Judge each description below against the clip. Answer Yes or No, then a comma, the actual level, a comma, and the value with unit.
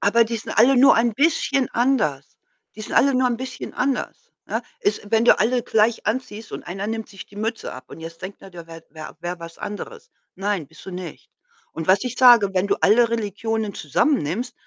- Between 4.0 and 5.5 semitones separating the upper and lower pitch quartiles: Yes, average, 4.8 semitones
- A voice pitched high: Yes, high, 220 Hz